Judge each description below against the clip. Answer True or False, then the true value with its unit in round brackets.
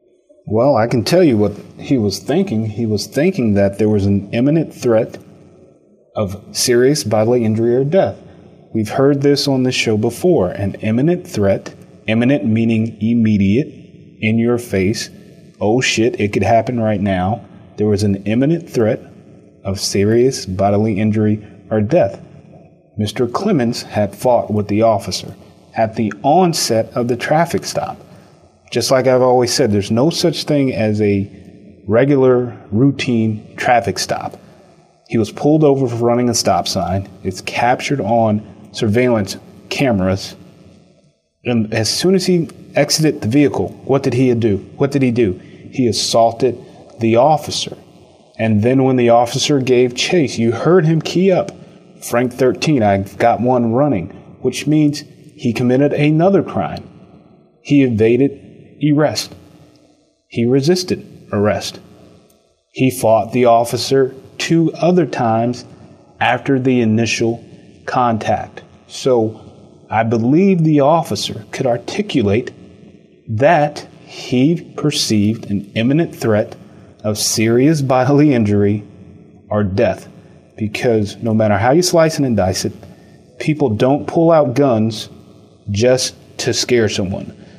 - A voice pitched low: True (115 Hz)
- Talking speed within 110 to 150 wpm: True (140 wpm)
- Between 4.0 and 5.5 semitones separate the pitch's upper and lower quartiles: True (4.6 semitones)